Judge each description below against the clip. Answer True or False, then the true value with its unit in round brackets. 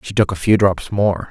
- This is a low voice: True (100 Hz)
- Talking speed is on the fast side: True (275 wpm)